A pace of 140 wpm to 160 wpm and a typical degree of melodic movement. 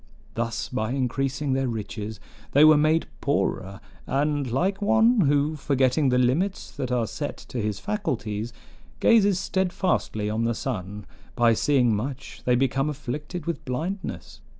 Yes: average, 145 wpm; average, 4.7 semitones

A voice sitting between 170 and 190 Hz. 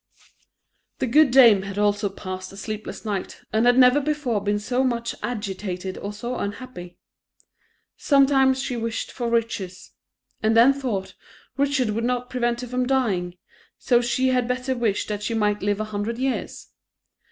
No: high, 235 Hz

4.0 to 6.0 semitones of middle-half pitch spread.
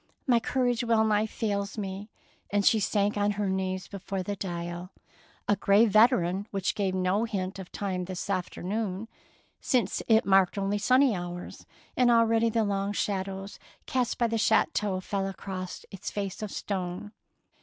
No: average, 2.7 semitones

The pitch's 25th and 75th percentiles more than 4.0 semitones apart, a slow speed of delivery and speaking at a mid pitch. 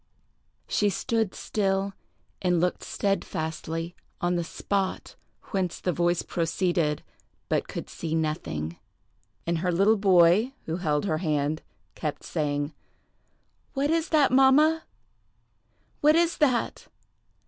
Yes: average, 5.2 semitones; slow, 115 wpm; medium, 180 Hz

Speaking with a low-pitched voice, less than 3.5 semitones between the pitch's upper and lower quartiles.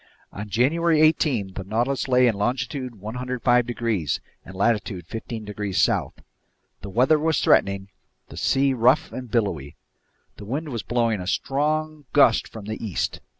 No: low, 120 Hz; average, 4.6 semitones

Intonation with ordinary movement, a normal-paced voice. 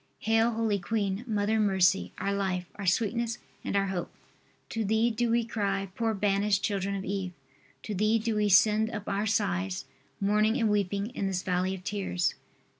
No: narrow, 2.3 semitones; average, 185 wpm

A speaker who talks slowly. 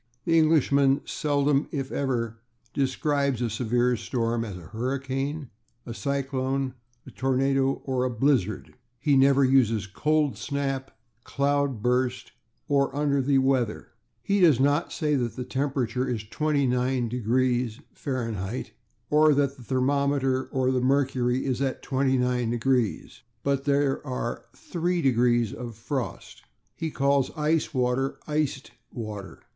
Yes: slow, 130 wpm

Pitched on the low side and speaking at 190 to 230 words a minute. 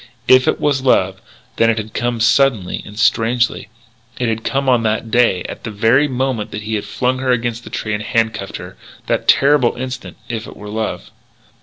Yes: low, 115 Hz; average, 195 wpm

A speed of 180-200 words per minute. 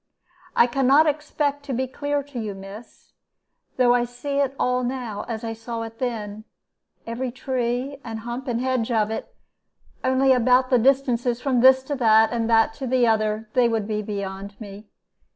Yes: average, 185 wpm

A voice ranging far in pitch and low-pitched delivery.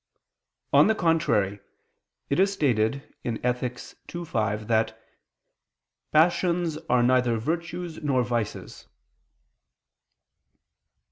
Yes: wide, 6.4 semitones; low, 130 Hz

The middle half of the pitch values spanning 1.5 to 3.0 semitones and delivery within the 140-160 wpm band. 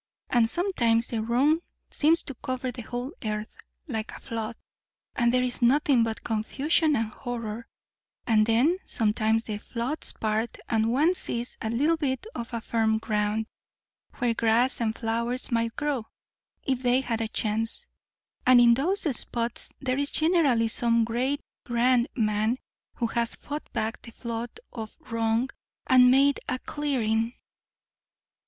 Yes: average, 2.7 semitones; average, 145 wpm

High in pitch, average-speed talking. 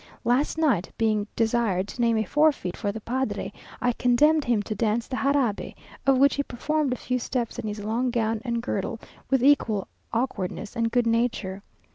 Yes: high, 235 Hz; average, 185 wpm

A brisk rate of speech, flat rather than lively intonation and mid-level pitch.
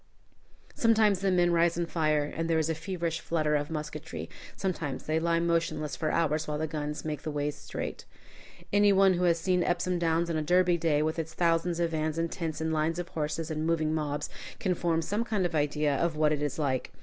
Yes: fast, 215 wpm; narrow, 2.1 semitones; medium, 160 Hz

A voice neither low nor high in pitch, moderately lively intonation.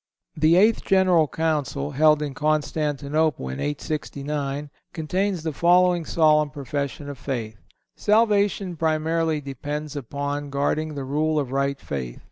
No: medium, 150 Hz; narrow, 2.3 semitones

